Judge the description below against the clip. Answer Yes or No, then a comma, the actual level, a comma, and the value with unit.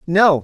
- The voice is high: No, medium, 170 Hz